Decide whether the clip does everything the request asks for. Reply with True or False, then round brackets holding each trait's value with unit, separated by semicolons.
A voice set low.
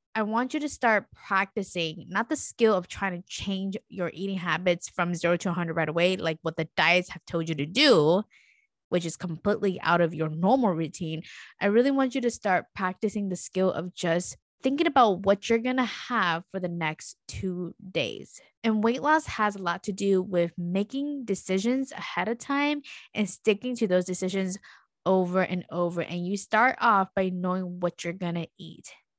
False (190 Hz)